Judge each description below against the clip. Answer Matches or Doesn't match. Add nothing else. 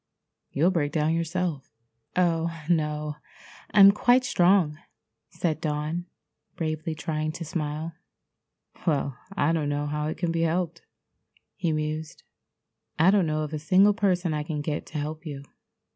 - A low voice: Doesn't match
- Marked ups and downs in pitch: Doesn't match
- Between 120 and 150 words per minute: Matches